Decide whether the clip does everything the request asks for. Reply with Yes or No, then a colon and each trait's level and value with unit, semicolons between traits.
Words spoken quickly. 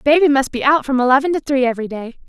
Yes: fast, 265 wpm